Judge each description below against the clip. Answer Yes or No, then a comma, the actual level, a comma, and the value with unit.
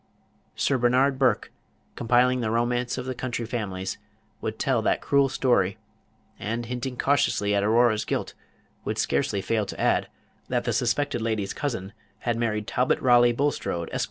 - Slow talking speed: No, average, 155 wpm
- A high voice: No, low, 120 Hz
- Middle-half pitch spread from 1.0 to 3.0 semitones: Yes, average, 2.7 semitones